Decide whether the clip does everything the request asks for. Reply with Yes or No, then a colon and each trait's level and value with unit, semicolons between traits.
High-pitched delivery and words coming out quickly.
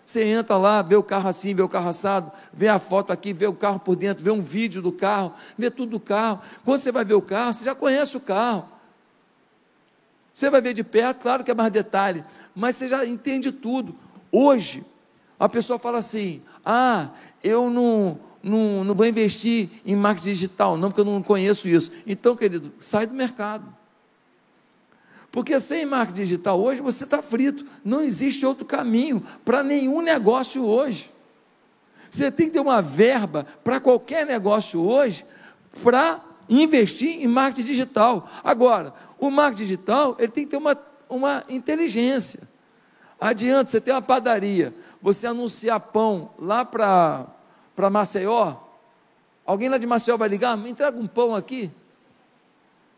No: high, 230 Hz; average, 165 wpm